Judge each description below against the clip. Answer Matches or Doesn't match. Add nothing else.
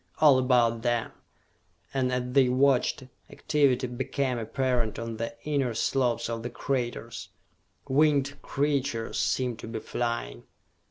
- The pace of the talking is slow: Matches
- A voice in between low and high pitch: Doesn't match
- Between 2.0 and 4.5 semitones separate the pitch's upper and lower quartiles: Matches